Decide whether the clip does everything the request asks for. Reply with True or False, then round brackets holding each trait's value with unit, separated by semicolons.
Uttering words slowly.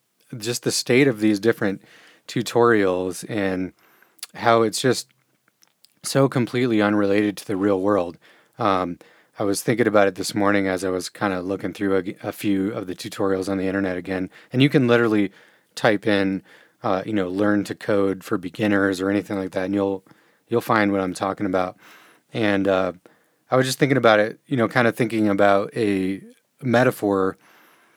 False (180 wpm)